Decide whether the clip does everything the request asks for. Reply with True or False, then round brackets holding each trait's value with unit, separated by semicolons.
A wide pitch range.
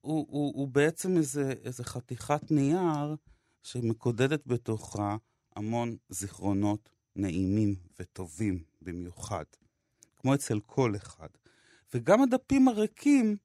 True (6.1 semitones)